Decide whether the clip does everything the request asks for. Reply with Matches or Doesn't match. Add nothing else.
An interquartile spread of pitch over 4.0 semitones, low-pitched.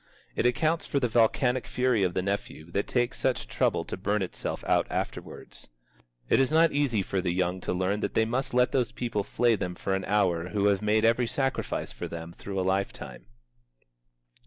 Matches